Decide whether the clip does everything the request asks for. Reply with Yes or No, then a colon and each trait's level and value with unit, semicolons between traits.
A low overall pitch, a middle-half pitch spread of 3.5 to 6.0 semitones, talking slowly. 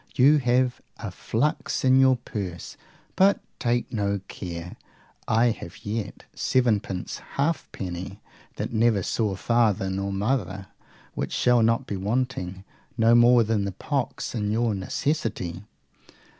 Yes: low, 110 Hz; average, 4.1 semitones; slow, 130 wpm